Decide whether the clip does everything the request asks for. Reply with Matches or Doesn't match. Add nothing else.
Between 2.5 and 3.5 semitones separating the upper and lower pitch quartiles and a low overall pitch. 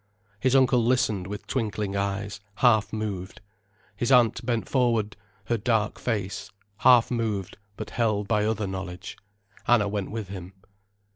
Matches